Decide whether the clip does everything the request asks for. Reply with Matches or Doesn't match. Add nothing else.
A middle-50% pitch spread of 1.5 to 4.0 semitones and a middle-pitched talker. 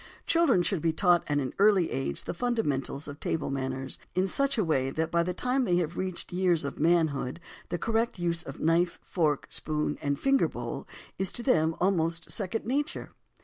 Doesn't match